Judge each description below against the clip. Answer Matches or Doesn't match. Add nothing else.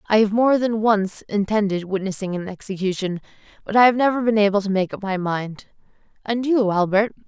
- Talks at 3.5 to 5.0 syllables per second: Doesn't match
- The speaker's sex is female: Matches